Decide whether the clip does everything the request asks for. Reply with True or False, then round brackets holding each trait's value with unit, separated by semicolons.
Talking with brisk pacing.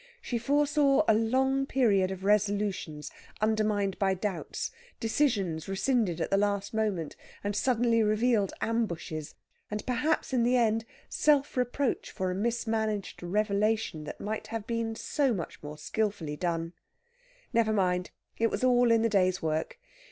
False (145 wpm)